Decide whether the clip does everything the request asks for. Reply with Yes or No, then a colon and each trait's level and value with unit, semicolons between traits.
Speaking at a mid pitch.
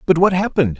Yes: medium, 165 Hz